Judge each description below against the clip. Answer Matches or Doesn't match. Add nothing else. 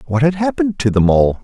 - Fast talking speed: Matches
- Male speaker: Matches